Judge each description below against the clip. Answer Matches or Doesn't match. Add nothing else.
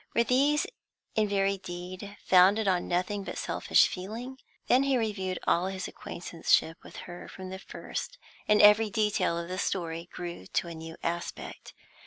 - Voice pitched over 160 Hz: Matches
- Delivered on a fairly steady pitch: Doesn't match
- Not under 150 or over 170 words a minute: Matches